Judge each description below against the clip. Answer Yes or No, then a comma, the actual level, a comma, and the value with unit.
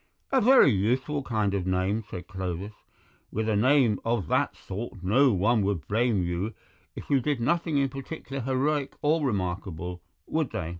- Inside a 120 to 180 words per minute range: Yes, average, 165 wpm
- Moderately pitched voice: No, low, 110 Hz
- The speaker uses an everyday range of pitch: No, wide, 6.4 semitones